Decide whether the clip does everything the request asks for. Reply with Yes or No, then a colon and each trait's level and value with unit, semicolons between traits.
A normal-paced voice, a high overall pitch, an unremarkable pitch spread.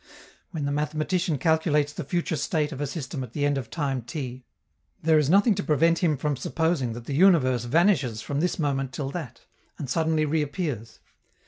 No: average, 195 wpm; medium, 150 Hz; average, 3.3 semitones